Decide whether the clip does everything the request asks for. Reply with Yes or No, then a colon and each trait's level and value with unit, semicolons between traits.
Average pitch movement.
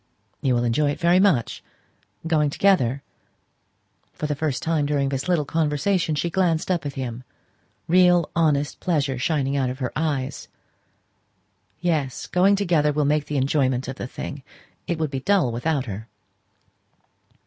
Yes: average, 3.7 semitones